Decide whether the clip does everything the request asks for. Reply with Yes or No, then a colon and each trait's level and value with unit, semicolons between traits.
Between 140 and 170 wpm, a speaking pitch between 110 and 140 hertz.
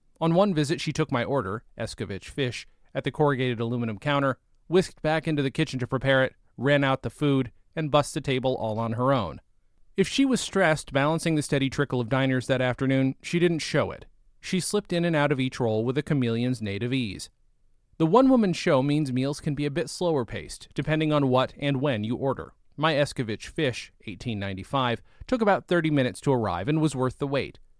No: fast, 205 wpm; low, 135 Hz